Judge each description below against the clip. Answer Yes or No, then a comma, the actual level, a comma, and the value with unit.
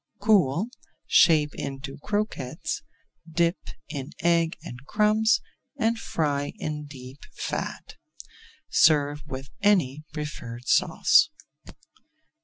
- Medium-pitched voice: Yes, medium, 150 Hz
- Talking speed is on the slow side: Yes, slow, 90 wpm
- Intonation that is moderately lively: No, wide, 6.6 semitones